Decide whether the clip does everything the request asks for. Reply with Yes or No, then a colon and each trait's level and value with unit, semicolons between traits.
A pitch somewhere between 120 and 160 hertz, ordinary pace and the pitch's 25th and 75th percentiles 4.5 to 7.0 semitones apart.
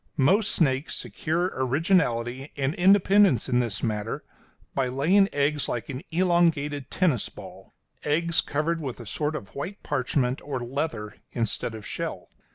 Yes: medium, 140 Hz; average, 145 wpm; average, 5.2 semitones